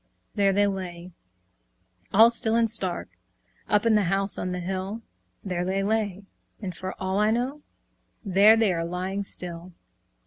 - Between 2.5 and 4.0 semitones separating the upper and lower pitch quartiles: Yes, average, 2.8 semitones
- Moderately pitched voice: No, high, 195 Hz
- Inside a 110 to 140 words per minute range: No, average, 160 wpm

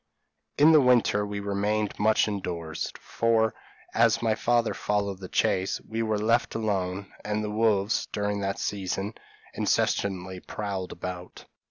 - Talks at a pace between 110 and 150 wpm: Yes, average, 140 wpm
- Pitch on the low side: Yes, low, 105 Hz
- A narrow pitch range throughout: Yes, narrow, 2.2 semitones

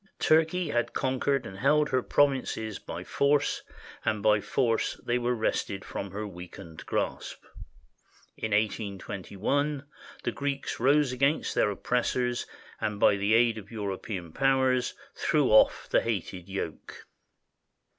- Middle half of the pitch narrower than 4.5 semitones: No, average, 5.1 semitones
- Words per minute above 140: No, slow, 135 wpm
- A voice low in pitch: Yes, low, 115 Hz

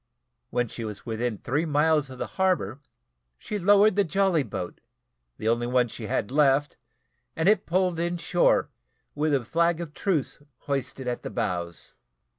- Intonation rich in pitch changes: Yes, wide, 6.1 semitones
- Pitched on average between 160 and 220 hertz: No, medium, 145 Hz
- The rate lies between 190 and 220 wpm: No, average, 165 wpm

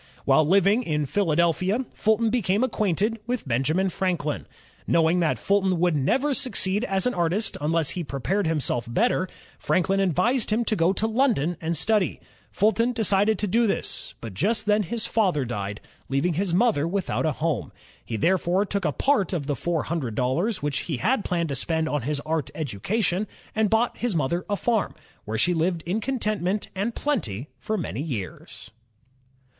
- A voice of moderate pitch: Yes, medium, 180 Hz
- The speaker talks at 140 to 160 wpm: No, average, 175 wpm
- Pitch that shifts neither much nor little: No, wide, 5.8 semitones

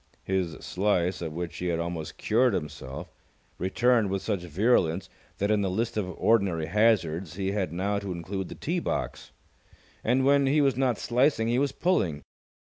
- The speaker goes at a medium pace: Yes, average, 175 wpm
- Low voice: Yes, low, 100 Hz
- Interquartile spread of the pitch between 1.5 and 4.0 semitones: No, average, 4.9 semitones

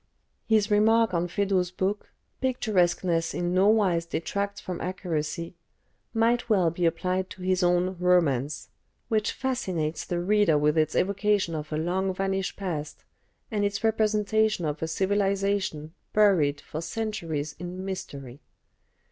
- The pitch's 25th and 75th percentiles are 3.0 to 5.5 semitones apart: Yes, average, 3.6 semitones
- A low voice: No, medium, 185 Hz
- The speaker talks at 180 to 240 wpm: No, slow, 135 wpm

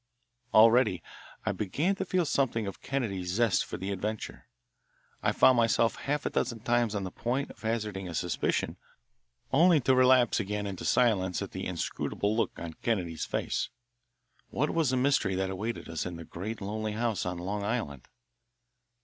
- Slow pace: No, average, 170 wpm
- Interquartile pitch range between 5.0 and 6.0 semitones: No, average, 4.5 semitones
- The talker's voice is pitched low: Yes, low, 110 Hz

